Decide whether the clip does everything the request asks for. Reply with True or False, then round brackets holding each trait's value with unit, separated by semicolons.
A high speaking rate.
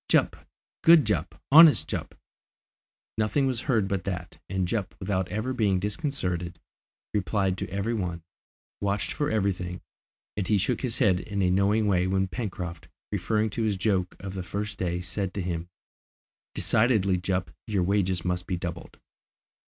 False (160 wpm)